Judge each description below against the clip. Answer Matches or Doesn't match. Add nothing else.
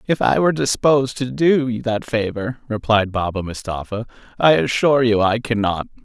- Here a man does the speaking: Matches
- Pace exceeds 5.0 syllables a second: Matches